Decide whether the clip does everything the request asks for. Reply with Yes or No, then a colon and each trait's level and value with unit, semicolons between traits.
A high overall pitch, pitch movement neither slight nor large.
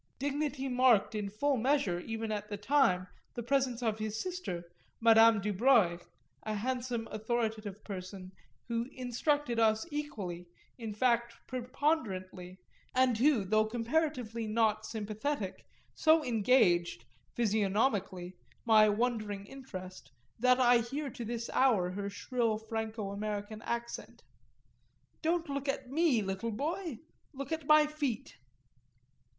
Yes: high, 230 Hz; average, 4.0 semitones